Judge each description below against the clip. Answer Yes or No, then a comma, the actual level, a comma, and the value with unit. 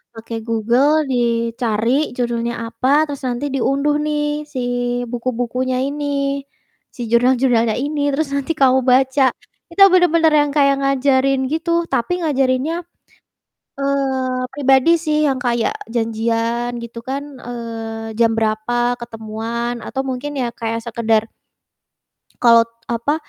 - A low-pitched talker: No, very high, 255 Hz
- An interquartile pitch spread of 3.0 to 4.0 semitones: Yes, average, 3.3 semitones